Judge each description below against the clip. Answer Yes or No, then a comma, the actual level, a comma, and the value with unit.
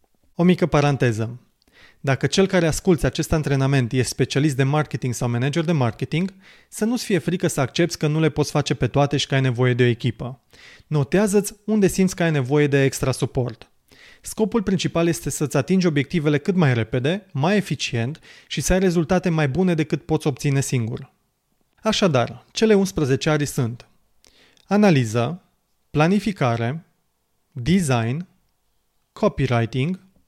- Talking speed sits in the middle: Yes, average, 150 wpm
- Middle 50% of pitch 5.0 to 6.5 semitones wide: Yes, average, 5.3 semitones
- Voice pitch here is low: No, medium, 150 Hz